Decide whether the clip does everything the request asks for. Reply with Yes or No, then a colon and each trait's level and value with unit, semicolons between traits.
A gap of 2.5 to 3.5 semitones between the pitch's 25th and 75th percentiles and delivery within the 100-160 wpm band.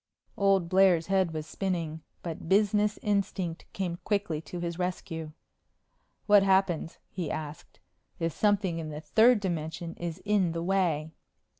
Yes: average, 3.1 semitones; average, 140 wpm